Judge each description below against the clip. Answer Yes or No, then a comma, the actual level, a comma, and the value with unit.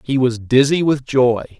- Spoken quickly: No, average, 190 wpm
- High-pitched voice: No, low, 130 Hz